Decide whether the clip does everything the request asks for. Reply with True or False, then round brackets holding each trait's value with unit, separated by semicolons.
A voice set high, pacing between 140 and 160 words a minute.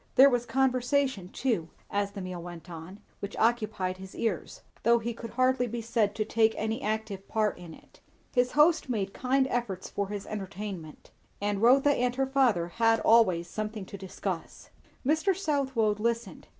False (220 Hz; 170 wpm)